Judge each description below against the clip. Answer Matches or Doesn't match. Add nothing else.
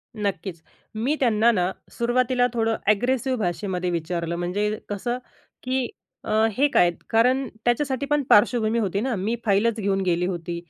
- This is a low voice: Doesn't match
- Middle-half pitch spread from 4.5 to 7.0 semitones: Matches